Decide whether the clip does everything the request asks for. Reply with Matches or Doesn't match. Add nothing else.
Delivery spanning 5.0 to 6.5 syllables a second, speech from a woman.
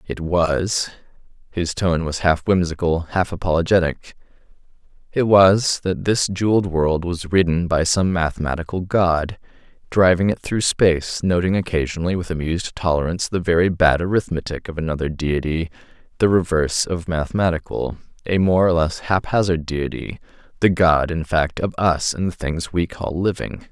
Doesn't match